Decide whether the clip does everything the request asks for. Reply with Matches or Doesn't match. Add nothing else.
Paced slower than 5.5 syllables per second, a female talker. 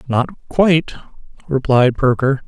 Doesn't match